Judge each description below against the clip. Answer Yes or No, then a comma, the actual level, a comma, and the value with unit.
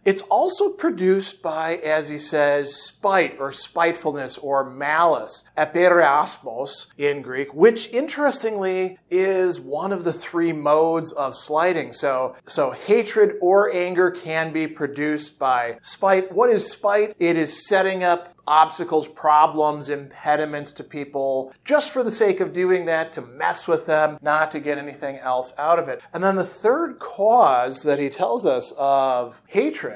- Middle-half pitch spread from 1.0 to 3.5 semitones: No, average, 4.5 semitones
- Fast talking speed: No, average, 155 wpm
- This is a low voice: No, medium, 160 Hz